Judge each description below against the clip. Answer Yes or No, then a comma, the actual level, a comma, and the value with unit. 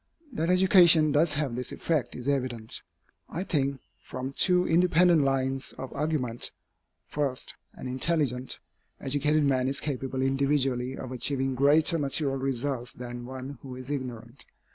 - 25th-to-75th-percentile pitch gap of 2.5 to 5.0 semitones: Yes, average, 2.8 semitones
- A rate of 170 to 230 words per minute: No, average, 140 wpm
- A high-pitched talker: No, low, 135 Hz